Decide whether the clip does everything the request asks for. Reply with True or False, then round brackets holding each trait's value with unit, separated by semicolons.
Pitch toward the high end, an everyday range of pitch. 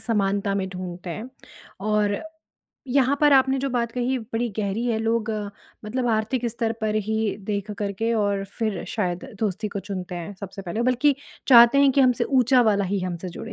True (220 Hz; 3.5 semitones)